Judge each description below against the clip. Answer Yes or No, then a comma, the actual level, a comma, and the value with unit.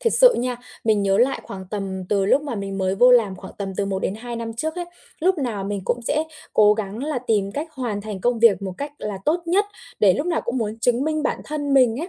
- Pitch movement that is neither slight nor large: No, wide, 6.1 semitones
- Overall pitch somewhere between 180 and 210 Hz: No, high, 230 Hz